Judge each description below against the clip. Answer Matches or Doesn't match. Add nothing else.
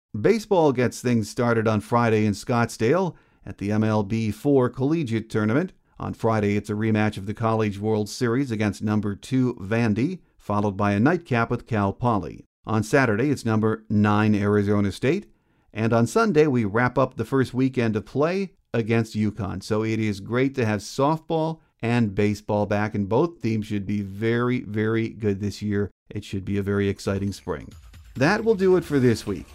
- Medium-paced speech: Matches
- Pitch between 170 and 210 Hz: Doesn't match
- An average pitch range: Matches